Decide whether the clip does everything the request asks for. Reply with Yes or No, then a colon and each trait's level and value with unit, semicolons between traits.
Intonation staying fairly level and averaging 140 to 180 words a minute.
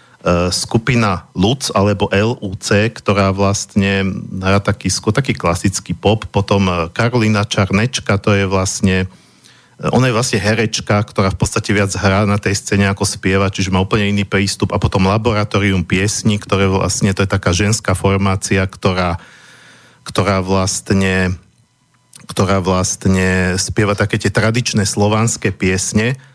No: narrow, 2.1 semitones; average, 130 wpm